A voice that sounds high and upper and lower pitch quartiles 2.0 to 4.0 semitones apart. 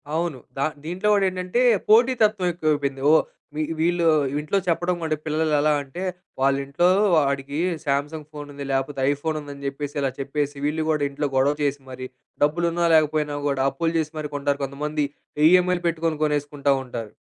No: medium, 150 Hz; average, 2.8 semitones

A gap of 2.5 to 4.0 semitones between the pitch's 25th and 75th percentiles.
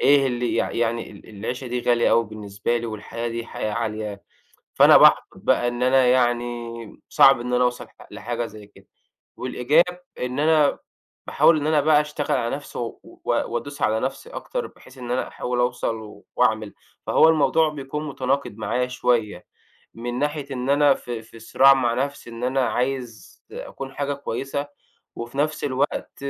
Yes: average, 3.2 semitones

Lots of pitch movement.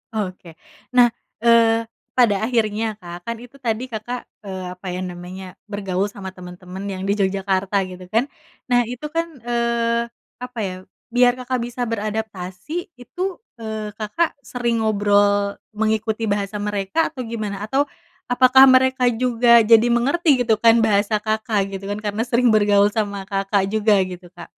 No: average, 3.2 semitones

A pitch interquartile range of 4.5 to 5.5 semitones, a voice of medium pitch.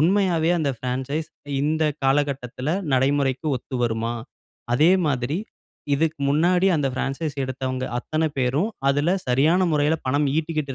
No: average, 3.4 semitones; medium, 145 Hz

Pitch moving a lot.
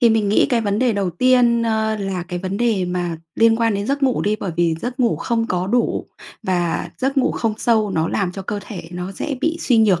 No: average, 4.1 semitones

